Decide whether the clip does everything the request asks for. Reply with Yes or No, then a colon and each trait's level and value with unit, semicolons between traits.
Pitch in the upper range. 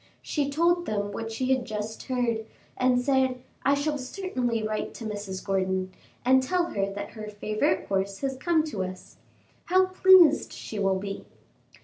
Yes: high, 245 Hz